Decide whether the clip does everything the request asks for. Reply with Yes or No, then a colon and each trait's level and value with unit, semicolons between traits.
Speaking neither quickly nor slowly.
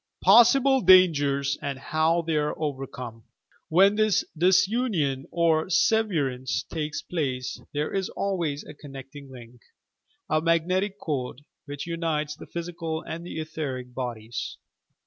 No: slow, 125 wpm